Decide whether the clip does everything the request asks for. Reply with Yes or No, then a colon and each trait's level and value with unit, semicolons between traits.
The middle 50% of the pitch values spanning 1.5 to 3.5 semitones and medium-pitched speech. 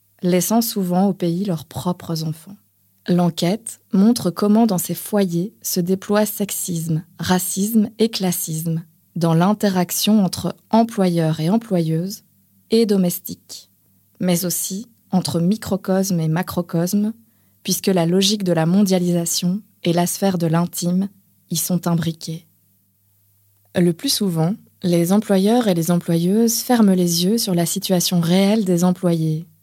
Yes: average, 2.9 semitones; medium, 180 Hz